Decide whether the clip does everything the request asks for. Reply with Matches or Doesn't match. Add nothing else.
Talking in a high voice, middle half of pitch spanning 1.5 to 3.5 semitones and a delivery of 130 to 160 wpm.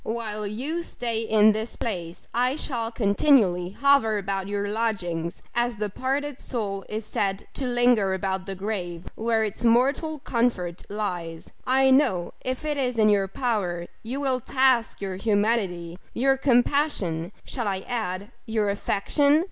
Doesn't match